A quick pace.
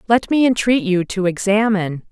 No: average, 170 wpm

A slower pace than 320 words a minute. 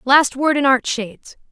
Yes: average, 200 wpm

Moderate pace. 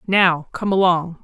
Yes: average, 145 wpm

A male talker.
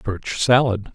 Yes: male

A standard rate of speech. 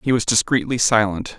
Yes: average, 175 wpm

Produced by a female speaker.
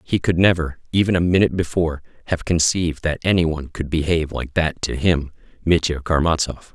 No: male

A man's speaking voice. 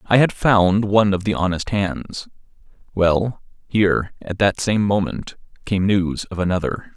Yes: male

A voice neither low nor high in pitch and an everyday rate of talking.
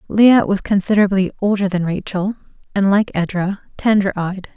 No: high, 195 Hz; average, 145 wpm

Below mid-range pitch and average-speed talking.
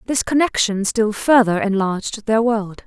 No: high, 220 Hz; average, 145 wpm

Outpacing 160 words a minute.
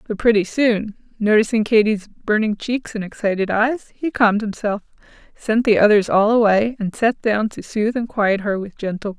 Yes: average, 190 wpm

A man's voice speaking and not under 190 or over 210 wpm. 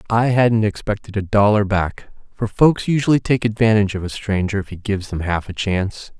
Yes: male; fast, 205 wpm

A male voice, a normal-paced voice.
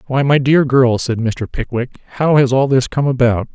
No: male; fast, 220 wpm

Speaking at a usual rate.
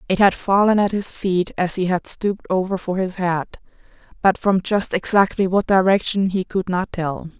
Yes: average, 185 wpm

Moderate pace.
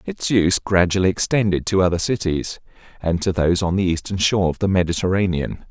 Yes: average, 180 wpm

